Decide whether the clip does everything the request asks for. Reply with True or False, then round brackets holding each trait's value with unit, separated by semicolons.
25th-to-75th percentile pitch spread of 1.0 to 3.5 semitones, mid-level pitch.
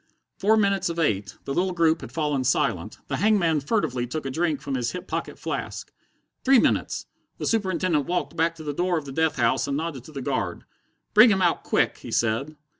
False (5.0 semitones; 160 Hz)